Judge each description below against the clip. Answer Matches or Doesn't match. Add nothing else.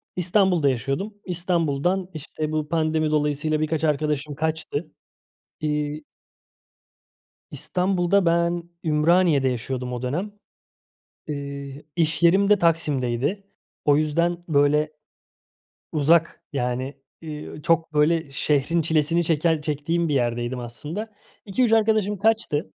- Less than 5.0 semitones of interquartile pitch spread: Matches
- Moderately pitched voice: Matches